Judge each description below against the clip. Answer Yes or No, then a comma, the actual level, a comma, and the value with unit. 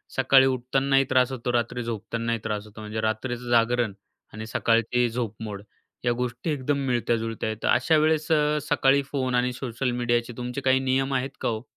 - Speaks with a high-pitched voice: No, low, 125 Hz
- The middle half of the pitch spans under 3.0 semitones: Yes, narrow, 2.6 semitones